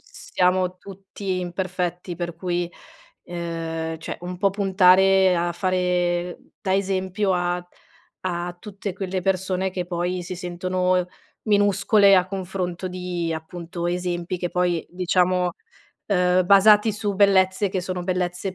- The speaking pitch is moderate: Yes, medium, 180 Hz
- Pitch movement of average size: No, narrow, 1.3 semitones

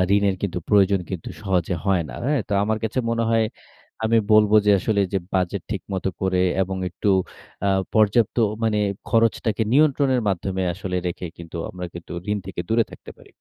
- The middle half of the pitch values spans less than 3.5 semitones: Yes, average, 3.1 semitones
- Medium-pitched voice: No, low, 100 Hz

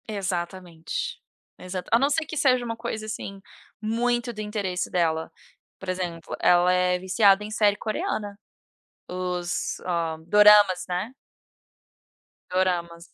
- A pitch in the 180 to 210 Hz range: Yes, high, 190 Hz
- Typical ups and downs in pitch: Yes, average, 3.2 semitones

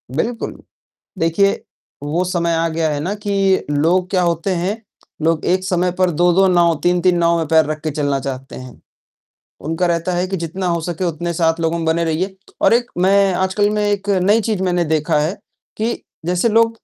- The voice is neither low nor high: Yes, medium, 175 Hz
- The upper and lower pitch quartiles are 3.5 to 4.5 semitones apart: No, average, 2.7 semitones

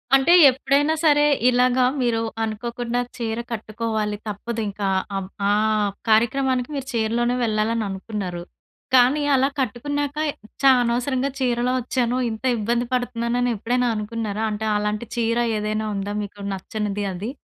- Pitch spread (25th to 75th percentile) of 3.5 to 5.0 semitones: No, average, 2.8 semitones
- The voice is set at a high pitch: Yes, high, 230 Hz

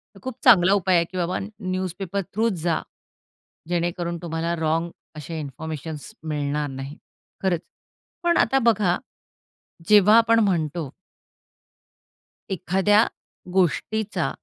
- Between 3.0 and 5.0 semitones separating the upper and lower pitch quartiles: Yes, average, 3.7 semitones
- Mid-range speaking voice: Yes, medium, 175 Hz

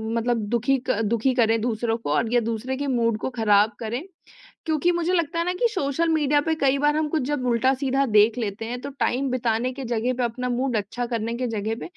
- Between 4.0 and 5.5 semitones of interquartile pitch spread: No, average, 3.5 semitones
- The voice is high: Yes, high, 245 Hz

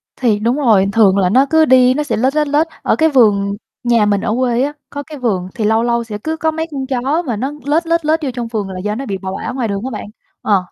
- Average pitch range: No, wide, 5.7 semitones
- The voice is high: Yes, high, 245 Hz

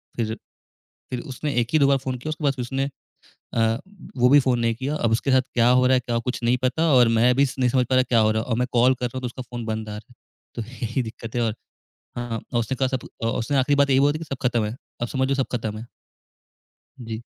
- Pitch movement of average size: No, narrow, 2.3 semitones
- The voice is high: No, low, 125 Hz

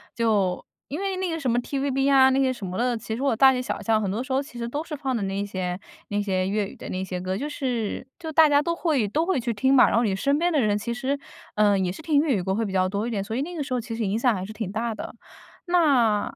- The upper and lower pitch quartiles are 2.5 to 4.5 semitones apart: No, wide, 5.4 semitones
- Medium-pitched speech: No, high, 235 Hz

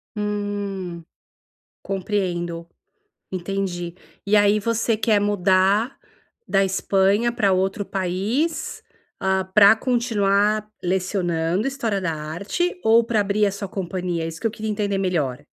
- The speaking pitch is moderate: No, high, 200 Hz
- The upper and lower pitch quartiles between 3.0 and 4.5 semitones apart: No, narrow, 2.6 semitones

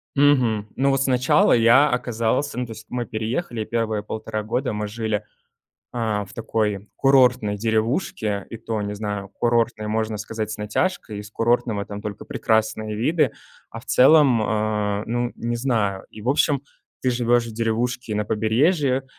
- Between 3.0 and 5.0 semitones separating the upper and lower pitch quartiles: No, narrow, 2.6 semitones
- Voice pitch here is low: Yes, low, 115 Hz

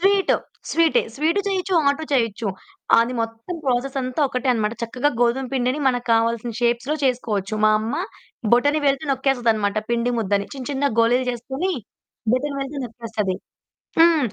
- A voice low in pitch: No, very high, 250 Hz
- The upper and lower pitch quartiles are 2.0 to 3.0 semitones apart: No, average, 3.6 semitones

